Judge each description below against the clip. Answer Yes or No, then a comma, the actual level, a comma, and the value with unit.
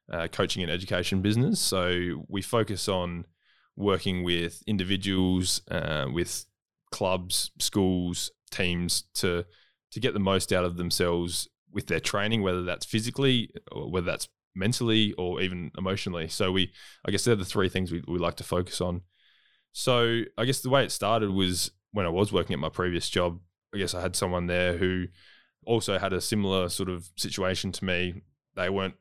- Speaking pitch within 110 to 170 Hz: No, very low, 95 Hz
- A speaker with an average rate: Yes, average, 180 wpm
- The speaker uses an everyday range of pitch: No, narrow, 2.3 semitones